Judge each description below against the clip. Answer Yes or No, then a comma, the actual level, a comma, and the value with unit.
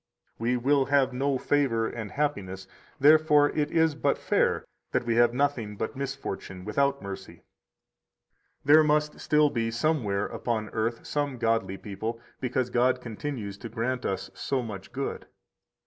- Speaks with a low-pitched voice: Yes, low, 125 Hz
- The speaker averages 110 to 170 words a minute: Yes, average, 150 wpm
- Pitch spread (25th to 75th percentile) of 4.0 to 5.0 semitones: Yes, average, 4.5 semitones